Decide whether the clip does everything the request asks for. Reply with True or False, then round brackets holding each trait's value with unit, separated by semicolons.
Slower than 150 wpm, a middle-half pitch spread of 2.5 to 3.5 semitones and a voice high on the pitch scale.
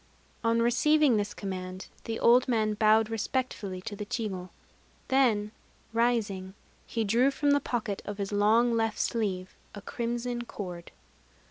True (140 wpm; 2.8 semitones; 225 Hz)